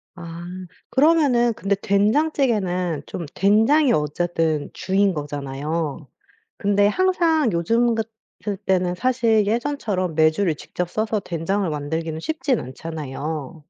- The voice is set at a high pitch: Yes, high, 195 Hz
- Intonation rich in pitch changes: Yes, wide, 6.1 semitones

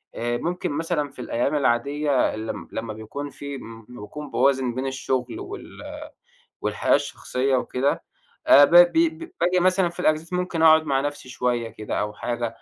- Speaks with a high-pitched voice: No, medium, 140 Hz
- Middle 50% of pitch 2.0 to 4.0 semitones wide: No, average, 5.1 semitones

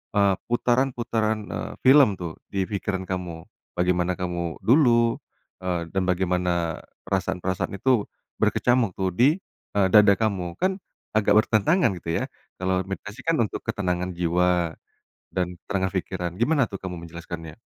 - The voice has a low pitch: Yes, very low, 95 Hz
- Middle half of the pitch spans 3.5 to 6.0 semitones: Yes, average, 3.9 semitones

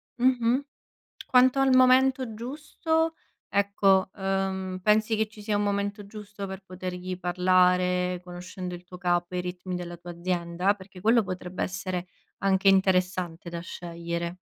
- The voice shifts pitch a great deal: No, average, 2.7 semitones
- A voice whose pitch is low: No, high, 190 Hz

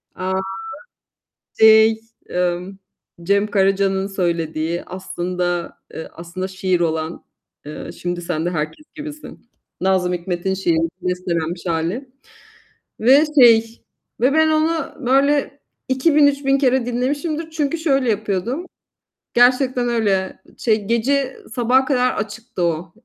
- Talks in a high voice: Yes, high, 210 Hz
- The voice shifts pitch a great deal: Yes, wide, 6.7 semitones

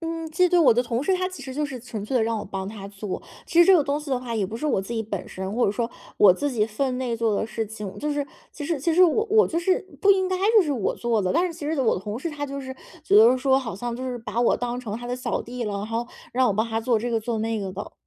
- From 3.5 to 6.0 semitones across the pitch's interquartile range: Yes, average, 5.0 semitones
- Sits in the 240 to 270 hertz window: Yes, high, 245 Hz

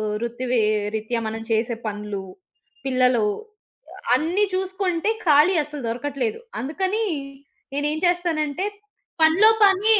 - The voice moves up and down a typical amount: No, wide, 7.4 semitones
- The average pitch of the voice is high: Yes, very high, 290 Hz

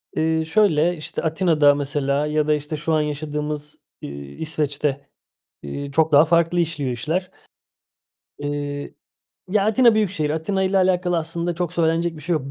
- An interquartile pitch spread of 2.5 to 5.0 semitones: Yes, average, 2.8 semitones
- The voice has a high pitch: No, medium, 155 Hz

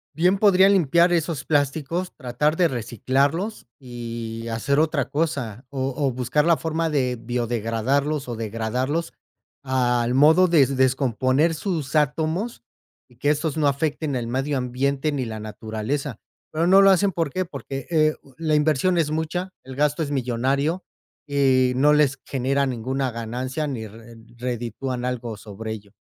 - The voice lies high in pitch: No, low, 135 Hz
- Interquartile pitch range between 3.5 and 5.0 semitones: Yes, average, 4.3 semitones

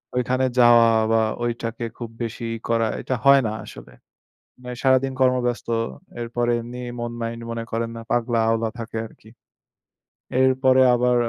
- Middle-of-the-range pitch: No, low, 120 Hz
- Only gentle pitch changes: Yes, narrow, 1.5 semitones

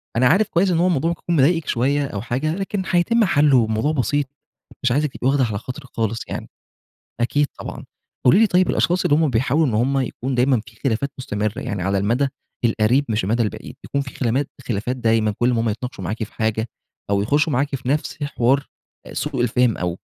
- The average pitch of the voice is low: Yes, low, 130 Hz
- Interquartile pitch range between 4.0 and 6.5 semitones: Yes, average, 4.5 semitones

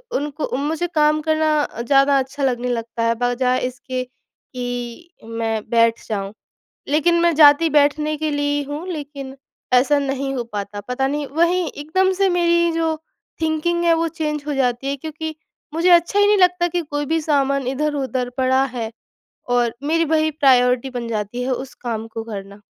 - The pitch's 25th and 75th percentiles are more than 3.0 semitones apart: Yes, average, 4.2 semitones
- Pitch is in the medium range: No, very high, 280 Hz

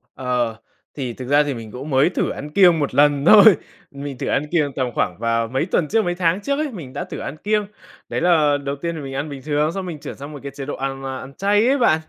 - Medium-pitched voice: Yes, medium, 145 Hz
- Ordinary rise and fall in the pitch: Yes, average, 4.5 semitones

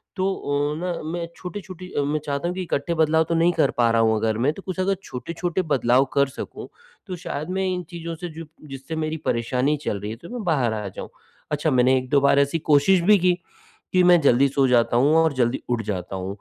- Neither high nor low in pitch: Yes, medium, 145 Hz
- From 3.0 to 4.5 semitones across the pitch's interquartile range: No, average, 5.2 semitones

